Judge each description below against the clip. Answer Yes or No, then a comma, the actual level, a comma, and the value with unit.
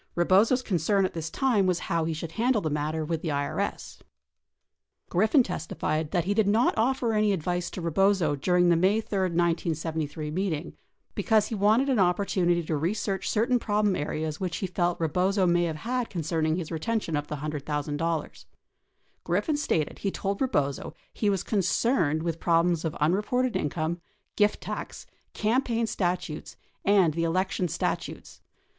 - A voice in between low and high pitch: Yes, medium, 180 Hz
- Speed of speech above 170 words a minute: No, average, 165 wpm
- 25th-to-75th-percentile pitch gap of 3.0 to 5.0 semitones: Yes, average, 4.5 semitones